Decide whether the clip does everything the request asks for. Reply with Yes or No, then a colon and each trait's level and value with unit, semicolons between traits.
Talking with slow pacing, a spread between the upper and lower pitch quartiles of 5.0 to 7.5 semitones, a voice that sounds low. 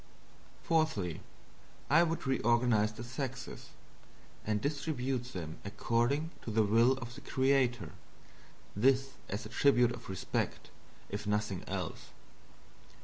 No: slow, 120 wpm; average, 4.3 semitones; low, 120 Hz